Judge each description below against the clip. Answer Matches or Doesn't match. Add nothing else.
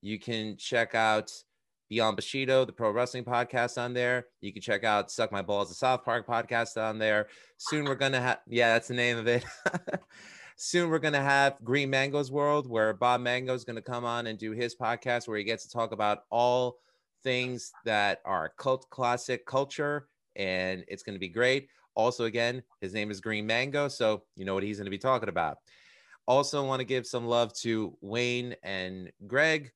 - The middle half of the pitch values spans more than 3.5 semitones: Doesn't match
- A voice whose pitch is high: Doesn't match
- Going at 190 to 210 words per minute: Matches